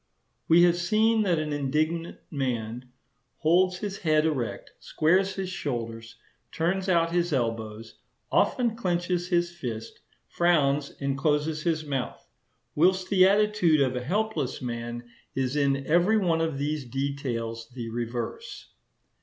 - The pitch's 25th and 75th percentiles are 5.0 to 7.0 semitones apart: Yes, wide, 5.5 semitones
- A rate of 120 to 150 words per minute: Yes, slow, 135 wpm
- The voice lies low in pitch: No, medium, 155 Hz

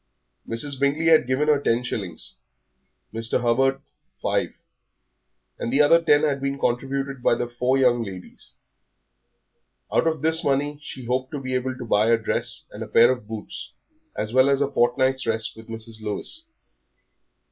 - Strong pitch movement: No, average, 3.2 semitones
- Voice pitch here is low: Yes, low, 130 Hz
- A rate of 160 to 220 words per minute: Yes, average, 170 wpm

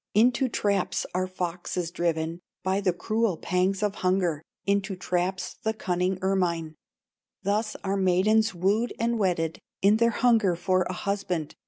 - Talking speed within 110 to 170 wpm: Yes, average, 145 wpm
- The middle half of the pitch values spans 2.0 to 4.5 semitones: Yes, average, 2.8 semitones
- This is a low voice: No, high, 190 Hz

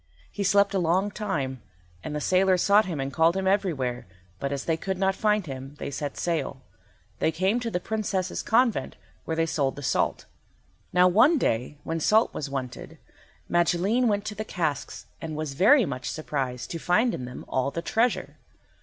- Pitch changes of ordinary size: No, wide, 6.2 semitones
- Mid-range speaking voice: Yes, medium, 175 Hz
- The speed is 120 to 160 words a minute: No, average, 190 wpm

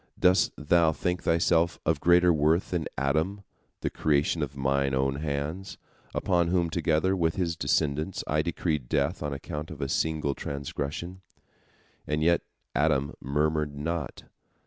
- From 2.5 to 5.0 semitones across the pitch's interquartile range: Yes, average, 3.1 semitones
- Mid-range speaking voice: No, very low, 80 Hz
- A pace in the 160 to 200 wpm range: No, average, 145 wpm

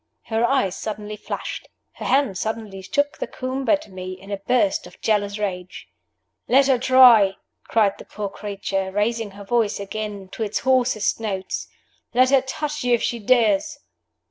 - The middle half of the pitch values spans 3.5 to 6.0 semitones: Yes, average, 4.4 semitones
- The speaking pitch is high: Yes, high, 215 Hz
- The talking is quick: No, average, 170 wpm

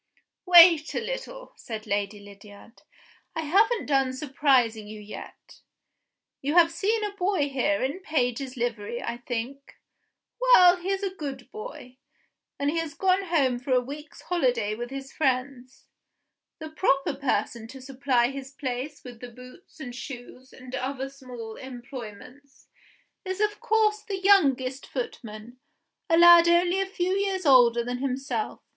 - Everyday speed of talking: Yes, average, 150 wpm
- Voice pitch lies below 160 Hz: No, very high, 275 Hz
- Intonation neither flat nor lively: No, wide, 5.9 semitones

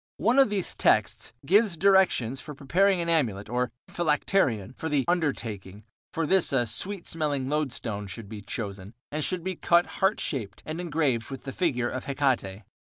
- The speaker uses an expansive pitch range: Yes, wide, 7.1 semitones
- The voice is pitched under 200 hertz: Yes, medium, 140 Hz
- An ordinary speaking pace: Yes, average, 175 wpm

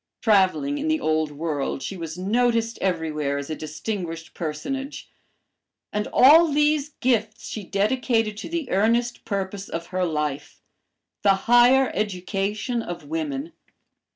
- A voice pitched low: No, high, 200 Hz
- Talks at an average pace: No, slow, 130 wpm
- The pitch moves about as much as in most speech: No, wide, 6.9 semitones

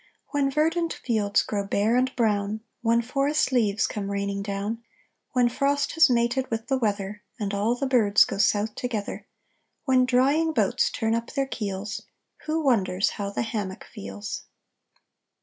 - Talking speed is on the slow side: No, average, 155 wpm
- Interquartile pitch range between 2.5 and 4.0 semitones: No, average, 4.6 semitones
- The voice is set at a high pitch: Yes, high, 230 Hz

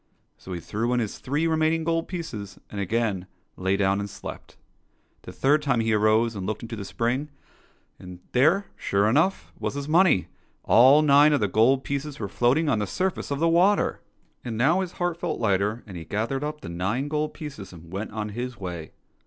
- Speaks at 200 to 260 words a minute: Yes, fast, 205 wpm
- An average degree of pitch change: No, wide, 6.8 semitones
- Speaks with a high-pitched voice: No, low, 120 Hz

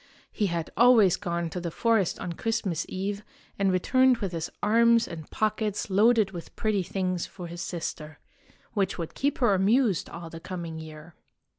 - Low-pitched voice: No, high, 190 Hz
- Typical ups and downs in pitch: Yes, average, 4.2 semitones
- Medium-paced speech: Yes, average, 170 wpm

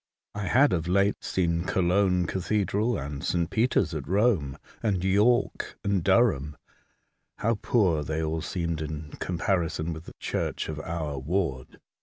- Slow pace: No, average, 145 wpm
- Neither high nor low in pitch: No, very low, 90 Hz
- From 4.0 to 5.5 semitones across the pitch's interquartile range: Yes, average, 4.3 semitones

